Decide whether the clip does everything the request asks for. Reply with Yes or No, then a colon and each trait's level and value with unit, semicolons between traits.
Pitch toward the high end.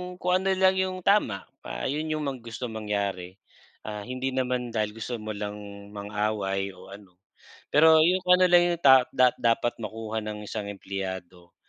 No: low, 115 Hz